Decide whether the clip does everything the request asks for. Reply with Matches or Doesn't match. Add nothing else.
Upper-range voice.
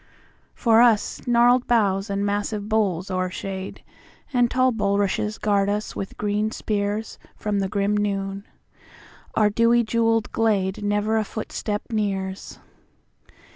Matches